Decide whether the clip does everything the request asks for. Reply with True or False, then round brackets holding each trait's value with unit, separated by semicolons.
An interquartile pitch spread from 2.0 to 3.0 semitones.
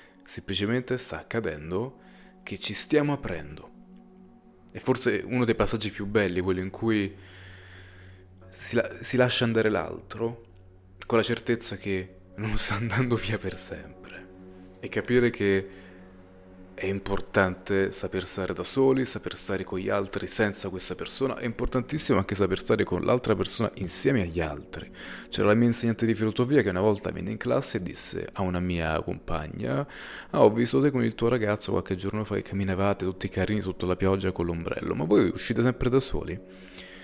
False (3.7 semitones)